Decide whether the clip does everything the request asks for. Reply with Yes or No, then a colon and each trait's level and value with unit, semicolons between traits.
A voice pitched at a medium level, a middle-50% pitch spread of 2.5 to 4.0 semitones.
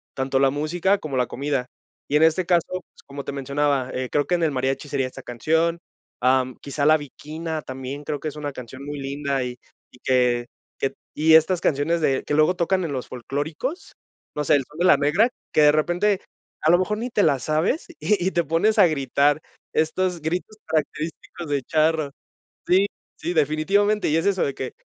Yes: medium, 150 Hz; average, 3.7 semitones